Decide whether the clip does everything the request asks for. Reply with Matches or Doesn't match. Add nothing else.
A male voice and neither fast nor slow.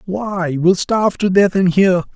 Matches